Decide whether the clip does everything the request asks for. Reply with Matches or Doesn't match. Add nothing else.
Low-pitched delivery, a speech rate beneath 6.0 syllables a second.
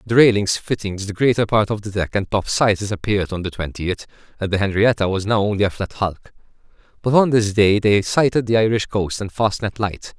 Matches